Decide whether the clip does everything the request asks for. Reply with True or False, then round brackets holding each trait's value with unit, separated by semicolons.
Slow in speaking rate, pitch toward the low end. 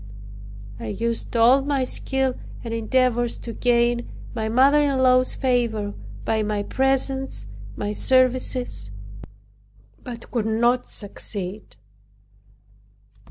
False (105 wpm; 240 Hz)